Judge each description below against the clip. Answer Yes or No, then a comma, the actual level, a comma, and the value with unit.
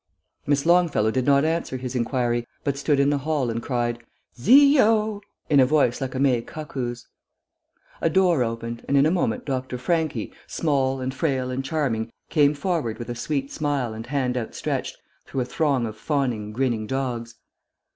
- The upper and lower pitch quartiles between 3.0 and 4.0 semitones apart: Yes, average, 3.7 semitones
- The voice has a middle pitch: No, low, 130 Hz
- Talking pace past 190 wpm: No, average, 175 wpm